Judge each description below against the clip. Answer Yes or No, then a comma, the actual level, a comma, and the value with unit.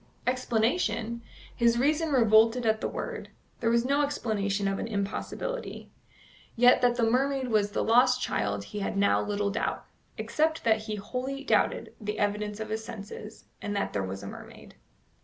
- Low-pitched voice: No, high, 225 Hz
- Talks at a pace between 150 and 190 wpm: Yes, average, 170 wpm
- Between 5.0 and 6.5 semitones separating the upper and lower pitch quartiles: No, average, 3.5 semitones